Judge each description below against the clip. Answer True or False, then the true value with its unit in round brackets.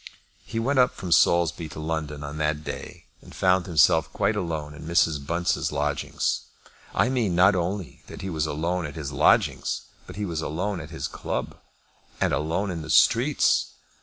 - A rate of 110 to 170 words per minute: False (180 wpm)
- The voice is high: False (80 Hz)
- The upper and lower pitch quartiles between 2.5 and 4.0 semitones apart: True (3.1 semitones)